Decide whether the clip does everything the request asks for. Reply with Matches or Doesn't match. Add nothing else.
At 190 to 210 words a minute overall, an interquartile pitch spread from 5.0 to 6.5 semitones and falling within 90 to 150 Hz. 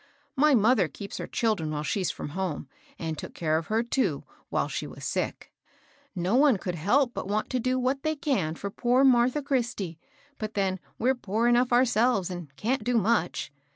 Doesn't match